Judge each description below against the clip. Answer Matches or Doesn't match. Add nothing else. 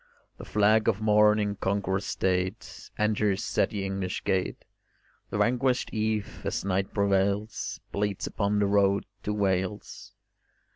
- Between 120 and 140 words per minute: Matches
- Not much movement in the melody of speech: Matches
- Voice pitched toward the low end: Matches